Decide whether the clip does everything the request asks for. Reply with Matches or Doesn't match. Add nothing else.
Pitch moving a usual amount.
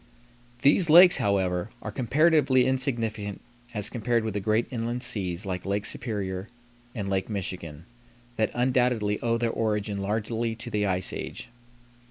Matches